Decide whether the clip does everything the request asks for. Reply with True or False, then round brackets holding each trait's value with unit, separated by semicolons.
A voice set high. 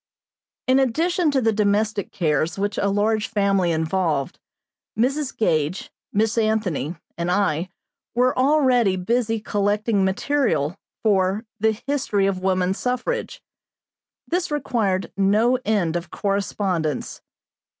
True (205 Hz)